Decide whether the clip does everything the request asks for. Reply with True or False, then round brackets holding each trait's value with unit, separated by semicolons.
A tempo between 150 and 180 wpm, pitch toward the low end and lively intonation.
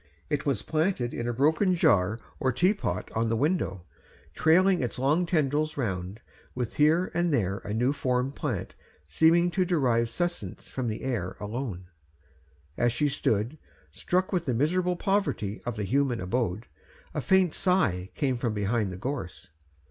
True (160 wpm; 130 Hz; 6.8 semitones)